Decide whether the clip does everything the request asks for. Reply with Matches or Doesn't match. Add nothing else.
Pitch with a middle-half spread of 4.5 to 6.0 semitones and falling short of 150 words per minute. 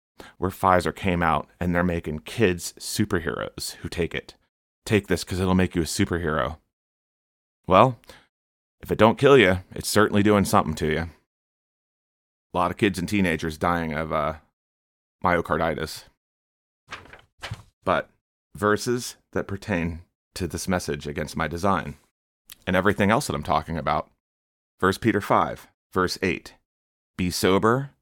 Doesn't match